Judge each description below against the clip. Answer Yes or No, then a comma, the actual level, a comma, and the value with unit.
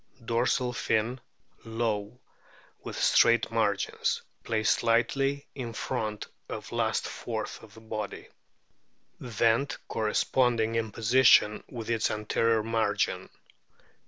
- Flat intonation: Yes, narrow, 1.8 semitones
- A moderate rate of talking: No, slow, 100 wpm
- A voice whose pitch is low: Yes, low, 115 Hz